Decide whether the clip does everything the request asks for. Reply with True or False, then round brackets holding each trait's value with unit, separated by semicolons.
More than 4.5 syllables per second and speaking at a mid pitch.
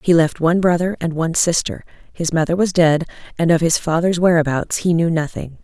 True (5.7 syllables/s; 165 Hz)